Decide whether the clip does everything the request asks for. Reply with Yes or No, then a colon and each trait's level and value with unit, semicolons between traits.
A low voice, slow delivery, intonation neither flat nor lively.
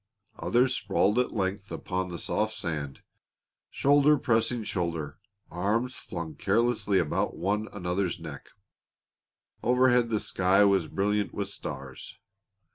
Yes: low, 100 Hz; slow, 120 wpm; average, 4.2 semitones